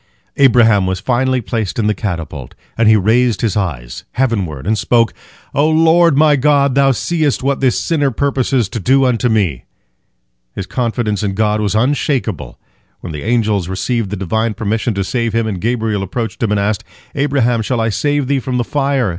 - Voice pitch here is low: Yes, low, 115 Hz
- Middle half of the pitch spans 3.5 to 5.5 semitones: Yes, average, 4.5 semitones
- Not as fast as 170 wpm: No, average, 185 wpm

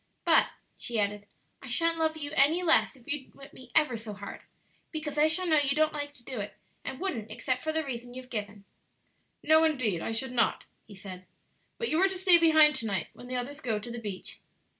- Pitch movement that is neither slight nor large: No, wide, 5.8 semitones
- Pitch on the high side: Yes, very high, 265 Hz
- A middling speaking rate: No, fast, 225 wpm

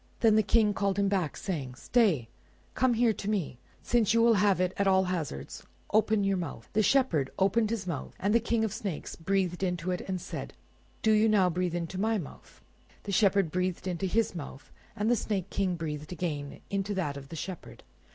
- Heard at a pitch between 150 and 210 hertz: Yes, high, 190 Hz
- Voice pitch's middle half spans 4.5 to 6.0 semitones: No, average, 3.6 semitones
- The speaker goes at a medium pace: No, fast, 210 wpm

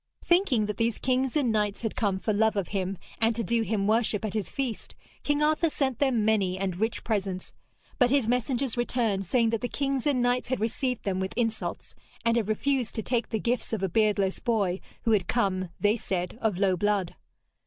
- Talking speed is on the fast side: Yes, fast, 210 wpm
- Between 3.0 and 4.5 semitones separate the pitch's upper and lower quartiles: Yes, average, 3.6 semitones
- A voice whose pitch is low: No, high, 225 Hz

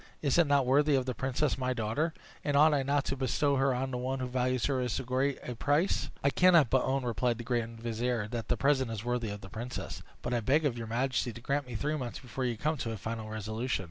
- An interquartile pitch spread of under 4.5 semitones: Yes, average, 3.0 semitones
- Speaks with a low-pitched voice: Yes, low, 130 Hz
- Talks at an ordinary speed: No, fast, 260 wpm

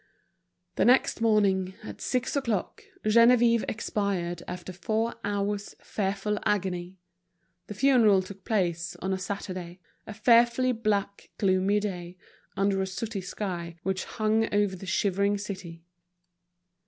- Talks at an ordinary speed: No, slow, 125 wpm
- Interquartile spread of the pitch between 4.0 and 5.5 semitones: No, narrow, 2.6 semitones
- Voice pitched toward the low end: No, high, 200 Hz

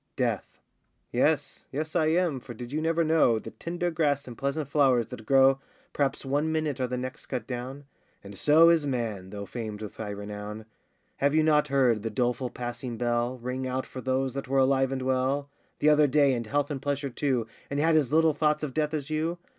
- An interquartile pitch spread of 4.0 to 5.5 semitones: No, average, 3.5 semitones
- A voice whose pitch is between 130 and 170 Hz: Yes, low, 135 Hz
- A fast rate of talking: Yes, fast, 210 wpm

